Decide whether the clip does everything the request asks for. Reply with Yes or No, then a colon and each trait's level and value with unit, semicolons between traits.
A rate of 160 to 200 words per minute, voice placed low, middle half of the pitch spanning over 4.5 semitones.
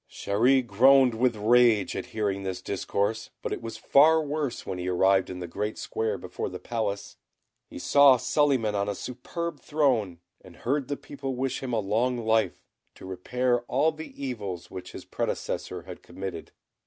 Yes: average, 175 wpm; low, 115 Hz; average, 5.2 semitones